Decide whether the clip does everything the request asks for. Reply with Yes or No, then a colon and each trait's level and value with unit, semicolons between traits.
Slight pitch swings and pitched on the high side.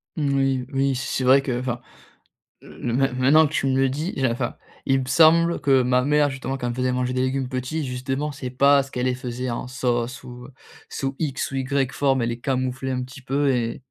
No: narrow, 1.4 semitones; low, 130 Hz